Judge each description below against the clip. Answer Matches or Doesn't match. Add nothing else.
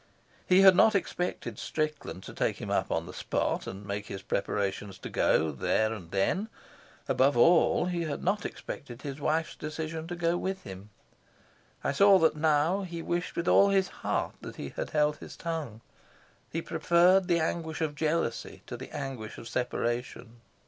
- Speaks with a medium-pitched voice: Matches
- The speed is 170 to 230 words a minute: Matches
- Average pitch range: Doesn't match